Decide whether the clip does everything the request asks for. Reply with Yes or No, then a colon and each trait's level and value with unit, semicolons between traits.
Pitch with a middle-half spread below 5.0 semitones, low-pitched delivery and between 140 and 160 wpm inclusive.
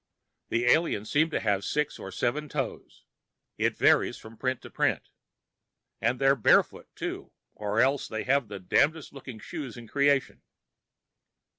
Yes: average, 4.4 semitones; low, 130 Hz; average, 150 wpm